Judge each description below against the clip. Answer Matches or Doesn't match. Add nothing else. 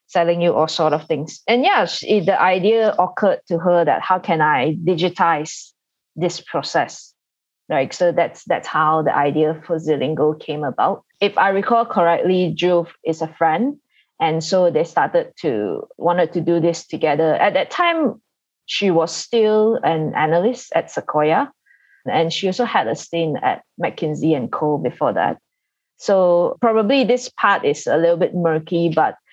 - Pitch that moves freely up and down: Matches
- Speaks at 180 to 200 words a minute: Doesn't match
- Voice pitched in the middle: Matches